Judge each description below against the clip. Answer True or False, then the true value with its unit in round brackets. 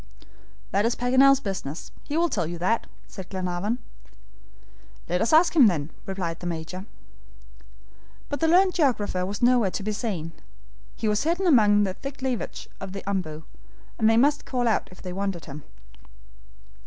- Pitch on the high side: True (205 Hz)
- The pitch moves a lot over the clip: True (6.0 semitones)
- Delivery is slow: False (160 wpm)